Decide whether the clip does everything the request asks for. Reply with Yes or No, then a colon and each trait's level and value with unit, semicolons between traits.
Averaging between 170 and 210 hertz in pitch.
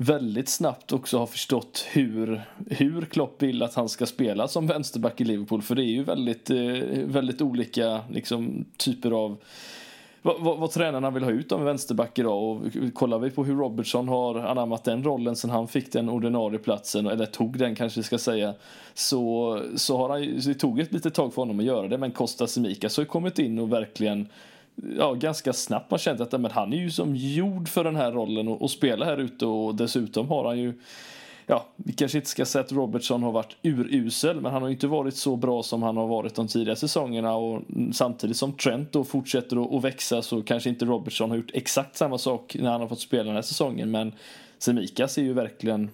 No: low, 120 Hz